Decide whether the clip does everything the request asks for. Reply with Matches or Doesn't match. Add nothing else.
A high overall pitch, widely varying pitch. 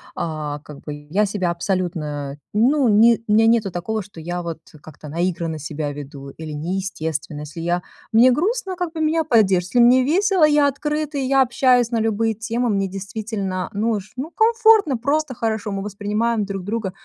Matches